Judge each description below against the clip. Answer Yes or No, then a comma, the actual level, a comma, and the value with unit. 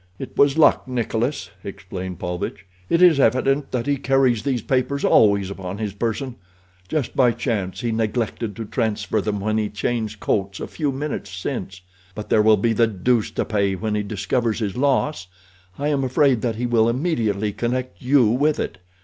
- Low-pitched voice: Yes, low, 115 Hz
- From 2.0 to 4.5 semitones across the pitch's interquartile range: Yes, average, 4.2 semitones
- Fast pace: No, average, 180 wpm